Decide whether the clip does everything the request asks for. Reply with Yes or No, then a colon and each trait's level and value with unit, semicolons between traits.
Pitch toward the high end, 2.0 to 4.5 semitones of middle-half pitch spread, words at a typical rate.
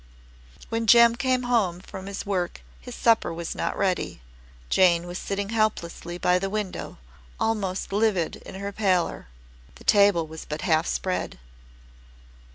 Yes: high, 195 Hz; average, 3.6 semitones; average, 145 wpm